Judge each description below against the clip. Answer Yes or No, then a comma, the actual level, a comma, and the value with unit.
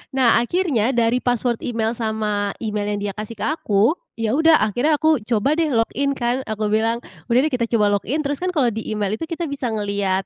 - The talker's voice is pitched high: Yes, high, 230 Hz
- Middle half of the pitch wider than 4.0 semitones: Yes, average, 4.4 semitones